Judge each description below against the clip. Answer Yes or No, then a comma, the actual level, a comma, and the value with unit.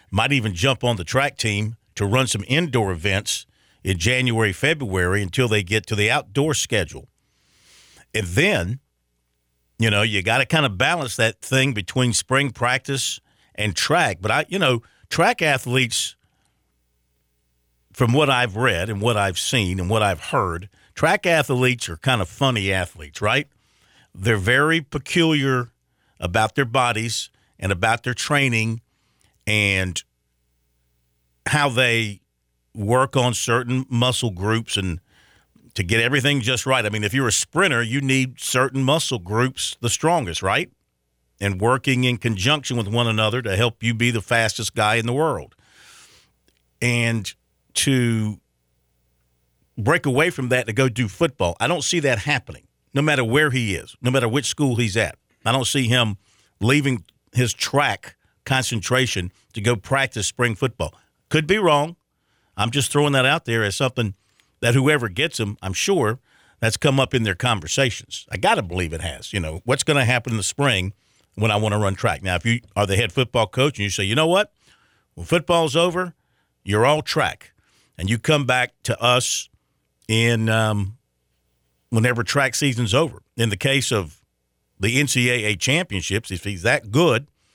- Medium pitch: No, low, 115 Hz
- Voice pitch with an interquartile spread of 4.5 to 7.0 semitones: Yes, average, 5.0 semitones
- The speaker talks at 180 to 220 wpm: No, average, 170 wpm